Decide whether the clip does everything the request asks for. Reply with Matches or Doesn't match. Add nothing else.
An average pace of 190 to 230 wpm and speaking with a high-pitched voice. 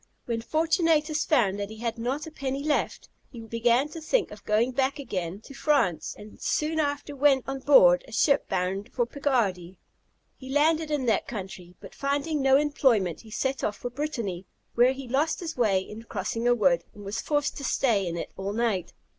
Matches